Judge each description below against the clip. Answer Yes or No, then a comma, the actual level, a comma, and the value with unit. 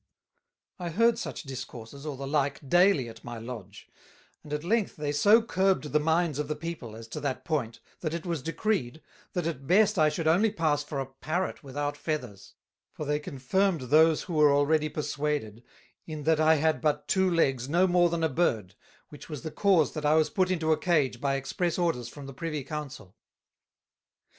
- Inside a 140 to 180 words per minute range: No, average, 195 wpm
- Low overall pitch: No, medium, 150 Hz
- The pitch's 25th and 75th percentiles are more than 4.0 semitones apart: No, average, 3.6 semitones